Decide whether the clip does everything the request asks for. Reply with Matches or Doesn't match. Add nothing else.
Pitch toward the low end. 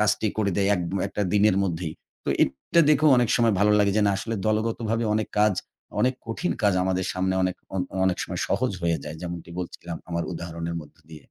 Matches